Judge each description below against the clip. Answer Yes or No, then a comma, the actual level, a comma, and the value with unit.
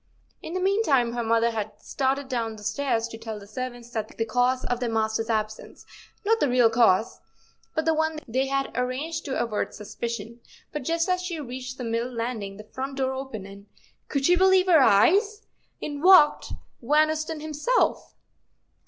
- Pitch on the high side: Yes, very high, 255 Hz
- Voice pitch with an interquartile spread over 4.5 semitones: Yes, wide, 5.4 semitones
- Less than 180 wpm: Yes, average, 160 wpm